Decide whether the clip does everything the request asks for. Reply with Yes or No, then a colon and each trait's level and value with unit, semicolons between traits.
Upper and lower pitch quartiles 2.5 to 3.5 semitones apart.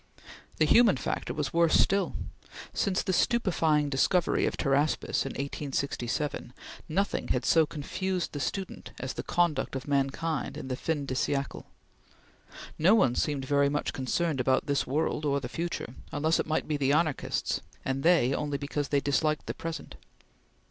Yes: average, 3.2 semitones